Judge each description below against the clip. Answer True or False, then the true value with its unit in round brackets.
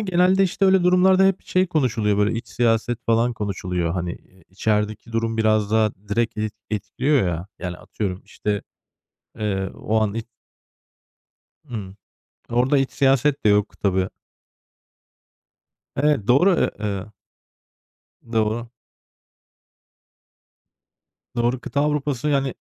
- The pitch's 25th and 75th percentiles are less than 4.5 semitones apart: False (5.1 semitones)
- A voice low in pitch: True (115 Hz)